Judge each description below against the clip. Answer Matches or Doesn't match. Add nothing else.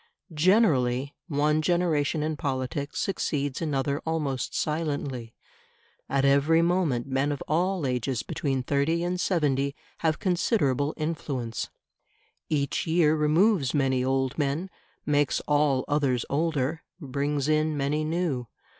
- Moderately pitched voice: Matches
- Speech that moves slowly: Matches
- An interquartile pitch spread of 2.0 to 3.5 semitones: Matches